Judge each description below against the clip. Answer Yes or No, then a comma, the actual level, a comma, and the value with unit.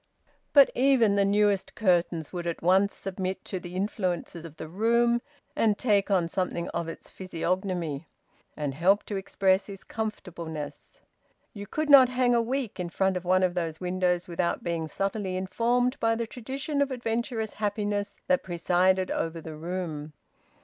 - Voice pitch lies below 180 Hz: No, high, 190 Hz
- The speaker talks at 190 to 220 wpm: No, average, 165 wpm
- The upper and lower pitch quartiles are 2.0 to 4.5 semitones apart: Yes, average, 4.1 semitones